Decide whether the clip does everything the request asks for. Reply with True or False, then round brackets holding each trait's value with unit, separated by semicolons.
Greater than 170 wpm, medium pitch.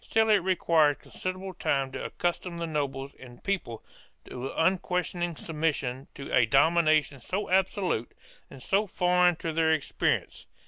False (140 wpm; 165 Hz)